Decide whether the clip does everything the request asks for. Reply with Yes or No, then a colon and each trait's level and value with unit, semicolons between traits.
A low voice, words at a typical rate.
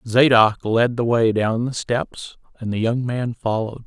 Yes: low, 115 Hz; average, 185 wpm